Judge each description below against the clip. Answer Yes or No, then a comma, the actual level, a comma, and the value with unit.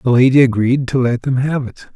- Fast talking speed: Yes, fast, 245 wpm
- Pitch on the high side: No, low, 130 Hz